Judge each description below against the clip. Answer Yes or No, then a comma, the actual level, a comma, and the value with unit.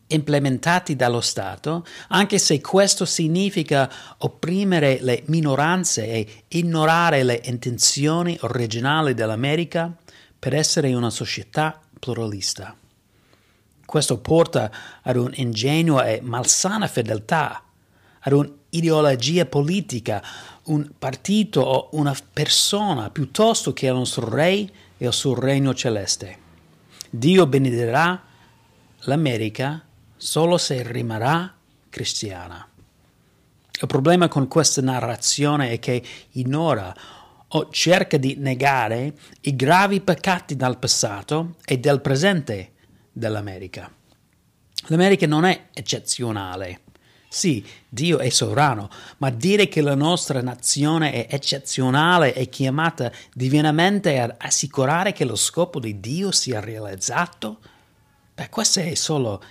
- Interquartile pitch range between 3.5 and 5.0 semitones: No, wide, 5.4 semitones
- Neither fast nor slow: No, slow, 110 wpm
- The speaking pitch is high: No, low, 135 Hz